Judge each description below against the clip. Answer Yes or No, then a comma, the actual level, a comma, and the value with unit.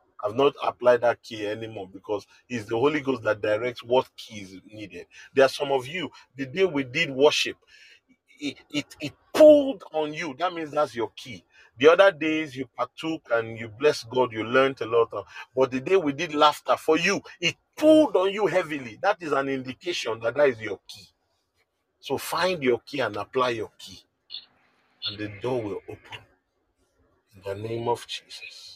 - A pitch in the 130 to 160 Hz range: Yes, low, 135 Hz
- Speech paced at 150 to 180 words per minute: No, average, 190 wpm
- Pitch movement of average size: No, wide, 6.4 semitones